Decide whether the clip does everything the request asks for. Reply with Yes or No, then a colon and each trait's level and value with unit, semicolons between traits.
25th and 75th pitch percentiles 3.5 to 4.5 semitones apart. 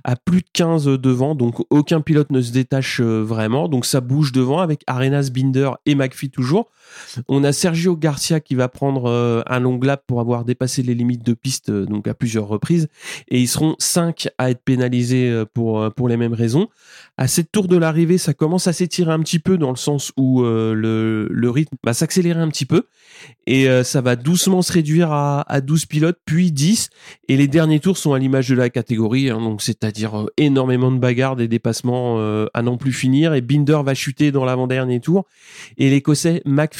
Yes: average, 4.2 semitones